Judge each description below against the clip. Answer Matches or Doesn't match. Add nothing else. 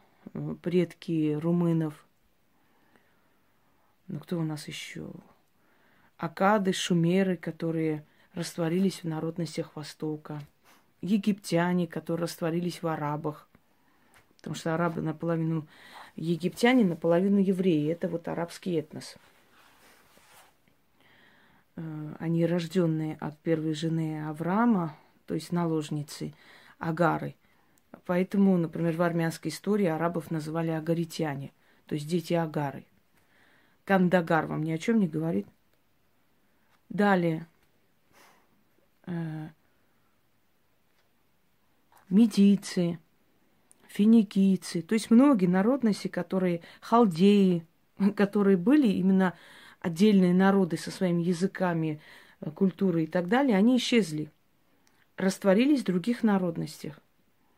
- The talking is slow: Matches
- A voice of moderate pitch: Matches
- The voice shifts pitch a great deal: Doesn't match